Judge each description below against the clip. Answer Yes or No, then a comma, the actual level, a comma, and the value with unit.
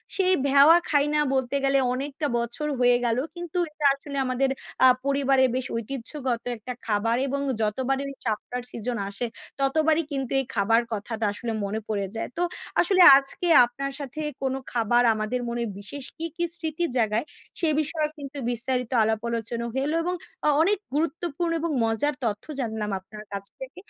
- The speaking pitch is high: Yes, very high, 260 Hz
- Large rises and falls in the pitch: No, average, 4.3 semitones